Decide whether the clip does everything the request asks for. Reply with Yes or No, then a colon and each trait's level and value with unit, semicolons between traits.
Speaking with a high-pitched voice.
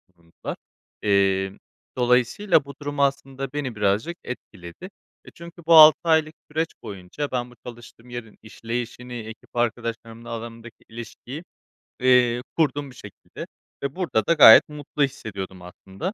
No: low, 120 Hz